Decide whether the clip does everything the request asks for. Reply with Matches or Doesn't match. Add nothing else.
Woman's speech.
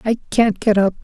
Doesn't match